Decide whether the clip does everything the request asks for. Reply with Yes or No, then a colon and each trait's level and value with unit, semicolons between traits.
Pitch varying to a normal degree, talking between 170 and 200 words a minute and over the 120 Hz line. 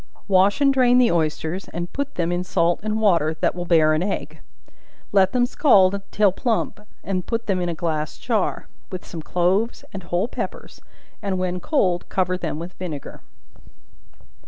Yes: average, 3.5 semitones; average, 175 wpm; medium, 185 Hz